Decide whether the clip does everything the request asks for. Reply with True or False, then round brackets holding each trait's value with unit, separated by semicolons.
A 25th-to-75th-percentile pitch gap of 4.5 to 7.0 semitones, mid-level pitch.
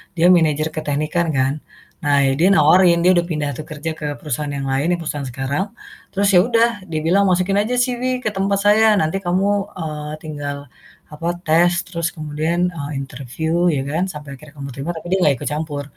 False (3.2 semitones; 155 Hz)